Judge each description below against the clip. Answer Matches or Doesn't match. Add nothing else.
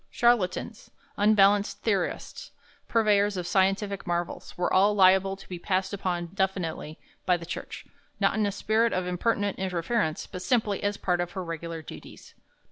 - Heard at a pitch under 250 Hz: Matches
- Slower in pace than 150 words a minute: Doesn't match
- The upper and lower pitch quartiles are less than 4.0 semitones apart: Matches